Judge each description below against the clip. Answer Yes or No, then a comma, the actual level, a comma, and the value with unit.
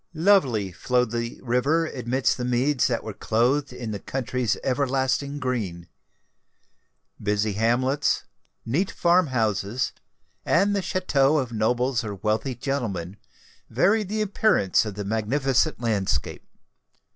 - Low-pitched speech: Yes, low, 125 Hz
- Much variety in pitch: No, average, 4.3 semitones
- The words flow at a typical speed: No, slow, 120 wpm